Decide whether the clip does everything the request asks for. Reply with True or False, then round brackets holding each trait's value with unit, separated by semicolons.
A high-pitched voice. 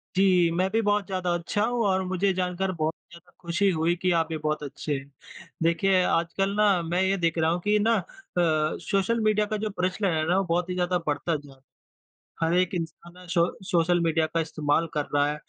False (175 Hz)